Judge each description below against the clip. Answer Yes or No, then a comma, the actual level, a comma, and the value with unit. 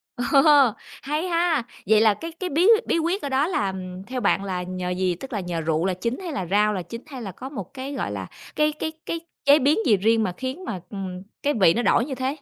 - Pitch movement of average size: No, wide, 7.5 semitones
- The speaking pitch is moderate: No, high, 235 Hz